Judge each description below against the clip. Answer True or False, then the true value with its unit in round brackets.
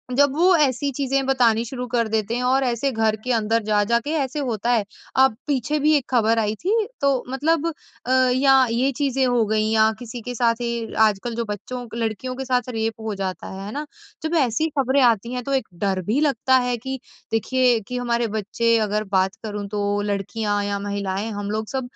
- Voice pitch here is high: True (235 Hz)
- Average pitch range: True (3.4 semitones)